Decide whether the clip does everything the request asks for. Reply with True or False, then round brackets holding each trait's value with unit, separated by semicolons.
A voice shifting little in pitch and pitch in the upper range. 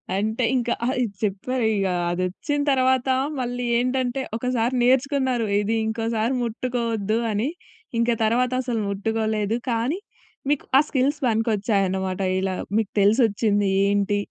False (3.5 semitones; 230 Hz)